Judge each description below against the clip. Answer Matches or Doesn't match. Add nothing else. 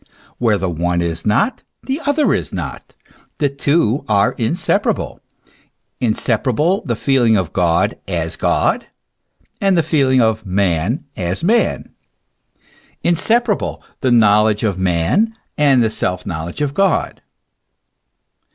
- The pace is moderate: Doesn't match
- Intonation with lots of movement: Matches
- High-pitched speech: Doesn't match